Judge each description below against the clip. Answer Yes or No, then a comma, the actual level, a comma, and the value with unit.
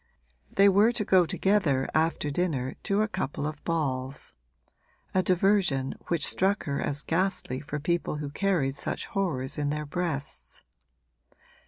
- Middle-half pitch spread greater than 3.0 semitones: Yes, average, 5.2 semitones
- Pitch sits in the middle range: Yes, medium, 160 Hz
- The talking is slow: No, average, 145 wpm